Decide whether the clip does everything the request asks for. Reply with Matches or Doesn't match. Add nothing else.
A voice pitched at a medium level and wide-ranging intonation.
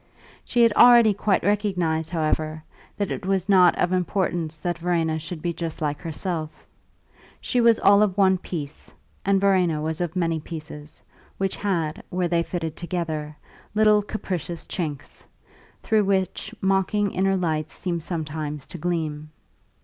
Doesn't match